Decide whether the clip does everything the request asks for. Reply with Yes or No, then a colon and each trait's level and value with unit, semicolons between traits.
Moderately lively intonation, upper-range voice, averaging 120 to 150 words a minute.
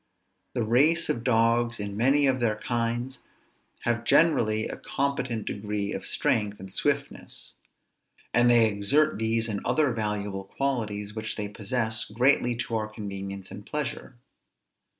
No: average, 3.2 semitones; low, 115 Hz; average, 140 wpm